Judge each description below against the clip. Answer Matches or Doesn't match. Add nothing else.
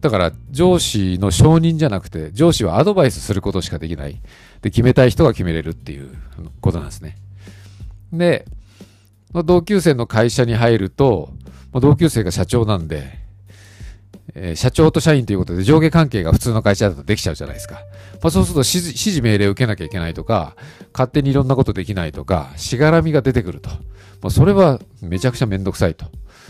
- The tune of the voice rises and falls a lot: Matches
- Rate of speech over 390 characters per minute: Matches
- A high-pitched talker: Doesn't match